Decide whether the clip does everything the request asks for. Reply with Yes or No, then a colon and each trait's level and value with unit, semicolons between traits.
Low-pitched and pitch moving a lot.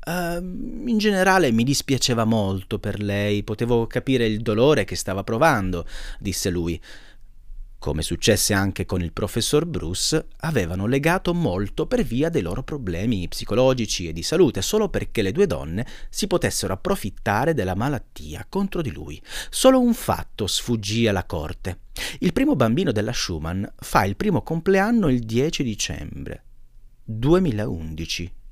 Yes: low, 115 Hz; wide, 8.1 semitones